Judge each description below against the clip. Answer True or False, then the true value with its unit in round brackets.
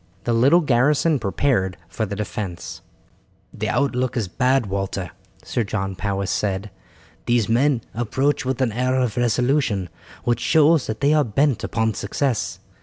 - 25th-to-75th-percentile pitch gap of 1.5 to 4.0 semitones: False (4.8 semitones)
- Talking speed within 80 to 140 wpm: False (150 wpm)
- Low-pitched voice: True (120 Hz)